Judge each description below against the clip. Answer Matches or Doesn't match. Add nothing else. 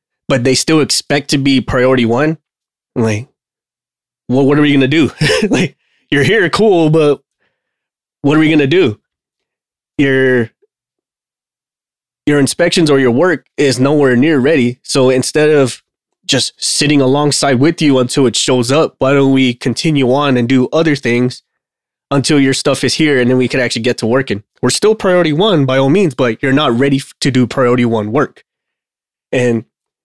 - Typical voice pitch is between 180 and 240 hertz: Doesn't match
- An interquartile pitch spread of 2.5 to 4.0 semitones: Matches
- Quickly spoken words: Doesn't match